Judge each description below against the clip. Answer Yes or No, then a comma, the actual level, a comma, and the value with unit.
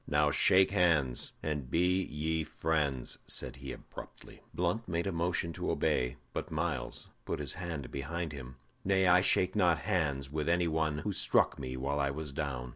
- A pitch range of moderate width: Yes, average, 3.9 semitones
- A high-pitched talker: No, very low, 80 Hz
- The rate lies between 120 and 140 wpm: No, average, 180 wpm